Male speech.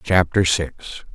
Yes: male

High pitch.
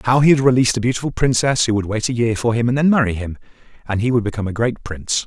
No: low, 115 Hz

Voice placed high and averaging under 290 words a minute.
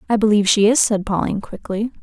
Yes: high, 210 Hz; fast, 205 wpm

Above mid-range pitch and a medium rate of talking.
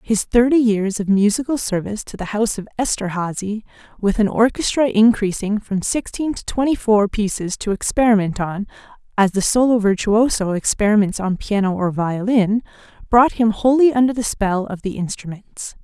Yes: high, 215 Hz; average, 160 wpm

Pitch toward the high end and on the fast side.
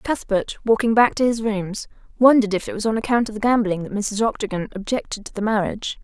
Yes: high, 215 Hz; fast, 220 wpm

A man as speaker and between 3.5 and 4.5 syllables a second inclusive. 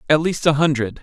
No: male; 6.0 syllables/s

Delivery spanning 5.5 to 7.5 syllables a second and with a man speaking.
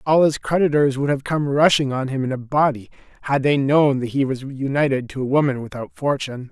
Yes: 5.7 syllables/s; male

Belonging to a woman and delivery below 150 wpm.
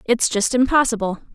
Yes: female; slow, 135 wpm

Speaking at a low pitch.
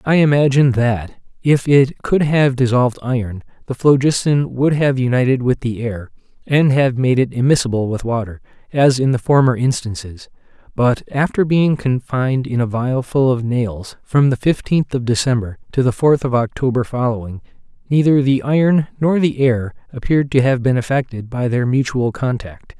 Yes: low, 130 Hz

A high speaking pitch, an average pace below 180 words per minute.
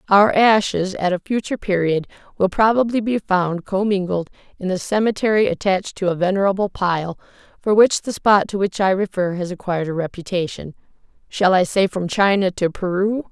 Yes: high, 195 Hz; average, 170 wpm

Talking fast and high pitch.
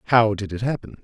No: fast, 230 wpm; low, 110 Hz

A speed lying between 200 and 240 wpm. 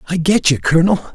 Yes: fast, 210 wpm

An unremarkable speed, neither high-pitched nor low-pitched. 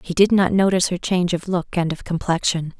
No: fast, 235 wpm; medium, 180 Hz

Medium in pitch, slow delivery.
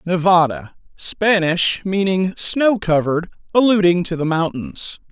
Yes: medium, 180 Hz; slow, 95 wpm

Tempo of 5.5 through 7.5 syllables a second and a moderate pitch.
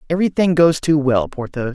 Yes: 5.7 syllables/s; medium, 150 Hz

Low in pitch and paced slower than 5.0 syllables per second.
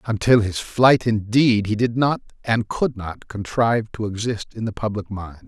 Yes: low, 110 Hz; 4.6 syllables/s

